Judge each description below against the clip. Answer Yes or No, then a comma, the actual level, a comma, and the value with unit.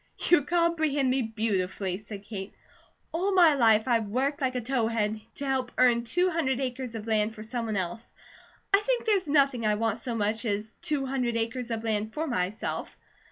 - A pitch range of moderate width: Yes, average, 4.1 semitones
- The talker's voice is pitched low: No, high, 235 Hz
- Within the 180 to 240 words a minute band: Yes, average, 185 wpm